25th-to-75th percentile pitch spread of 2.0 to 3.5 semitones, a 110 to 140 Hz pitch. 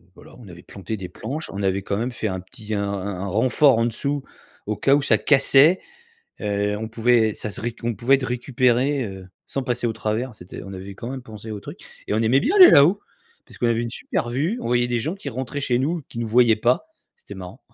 No: average, 4.0 semitones; low, 120 Hz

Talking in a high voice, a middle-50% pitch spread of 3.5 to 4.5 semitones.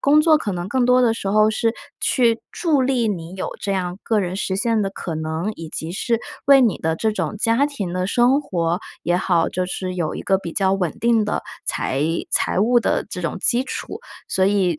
No: high, 200 Hz; average, 4.9 semitones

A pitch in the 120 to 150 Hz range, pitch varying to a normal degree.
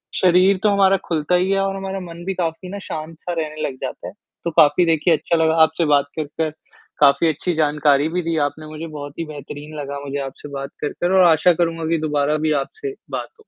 No: medium, 160 Hz; average, 3.3 semitones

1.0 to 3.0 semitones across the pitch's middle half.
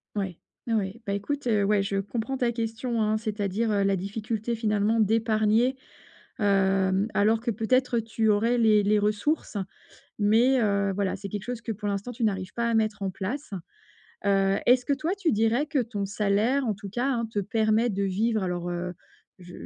Yes: average, 2.7 semitones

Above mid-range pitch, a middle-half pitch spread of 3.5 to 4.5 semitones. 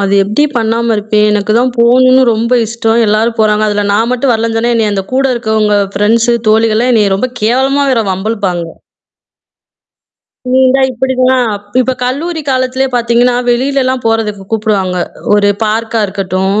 No: high, 225 Hz; average, 3.1 semitones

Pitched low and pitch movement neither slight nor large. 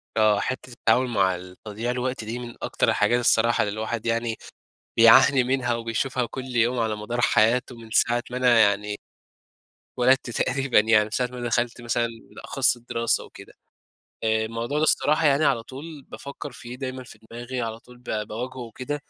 No: low, 120 Hz; narrow, 2.2 semitones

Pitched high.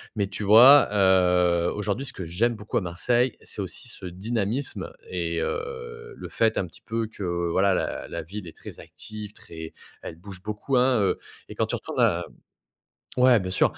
No: low, 105 Hz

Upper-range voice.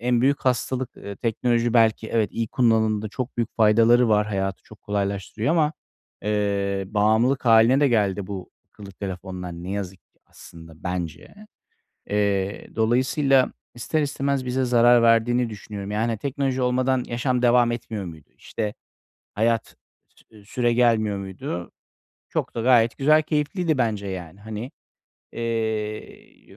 No: low, 115 Hz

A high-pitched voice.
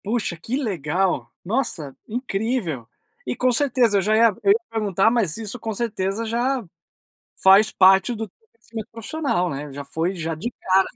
Yes: high, 210 Hz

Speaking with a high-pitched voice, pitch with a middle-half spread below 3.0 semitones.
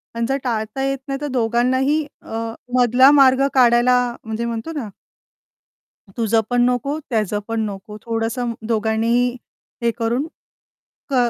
Yes: high, 240 Hz; narrow, 2.6 semitones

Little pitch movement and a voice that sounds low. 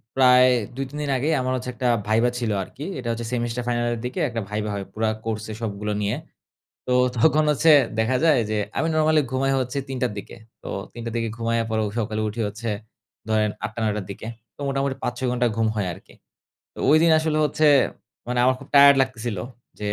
No: average, 3.3 semitones; low, 120 Hz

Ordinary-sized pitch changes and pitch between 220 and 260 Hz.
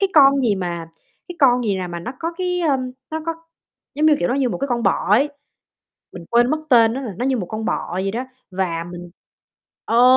No: wide, 6.4 semitones; high, 245 Hz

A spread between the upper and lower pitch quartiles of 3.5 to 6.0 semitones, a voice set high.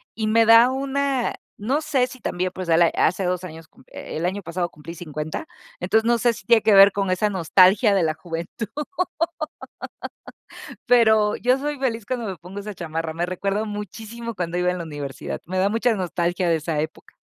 Yes: average, 4.9 semitones; high, 195 Hz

